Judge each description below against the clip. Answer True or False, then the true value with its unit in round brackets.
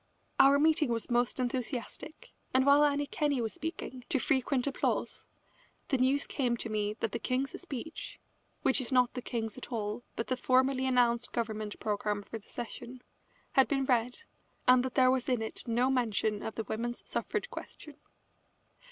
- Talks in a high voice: True (250 Hz)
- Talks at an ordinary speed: True (175 wpm)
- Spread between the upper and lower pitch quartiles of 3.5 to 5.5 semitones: False (2.7 semitones)